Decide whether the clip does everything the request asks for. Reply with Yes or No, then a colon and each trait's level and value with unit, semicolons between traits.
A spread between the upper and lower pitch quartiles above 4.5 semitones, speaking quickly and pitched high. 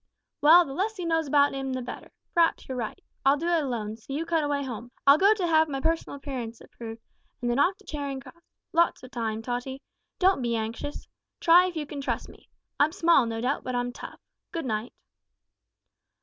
Yes: average, 5.1 semitones; fast, 210 wpm; very high, 280 Hz